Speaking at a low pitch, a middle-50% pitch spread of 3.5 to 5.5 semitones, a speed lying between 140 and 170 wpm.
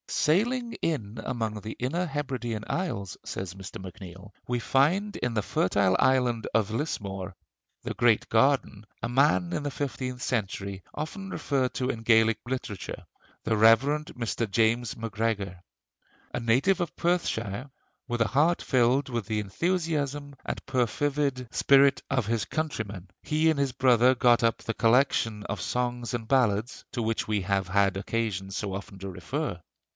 Yes: low, 120 Hz; average, 4.9 semitones; average, 155 wpm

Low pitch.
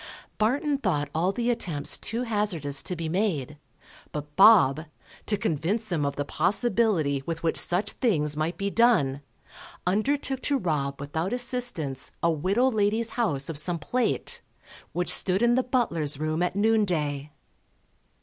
No: medium, 180 Hz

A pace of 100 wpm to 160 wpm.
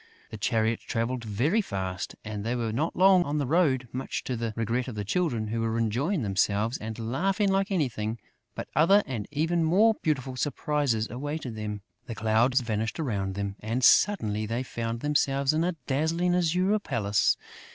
No: average, 175 wpm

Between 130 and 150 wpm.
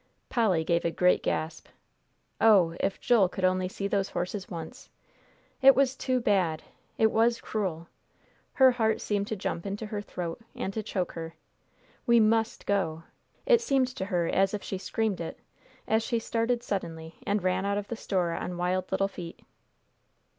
No: average, 175 wpm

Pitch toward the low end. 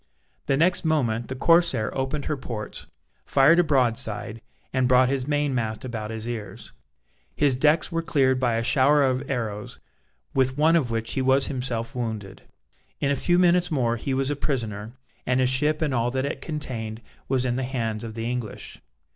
Yes: low, 130 Hz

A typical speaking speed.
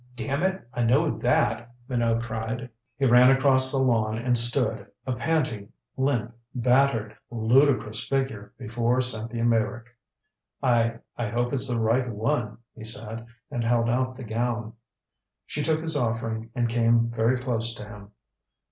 Yes: average, 150 wpm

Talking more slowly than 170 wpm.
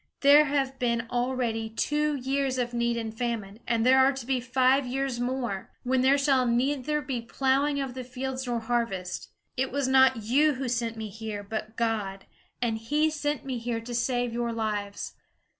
No: average, 180 wpm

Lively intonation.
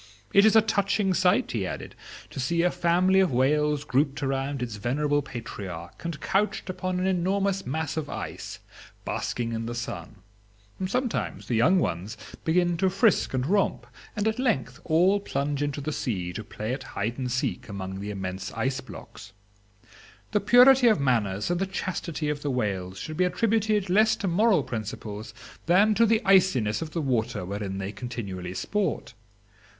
Yes: wide, 8.8 semitones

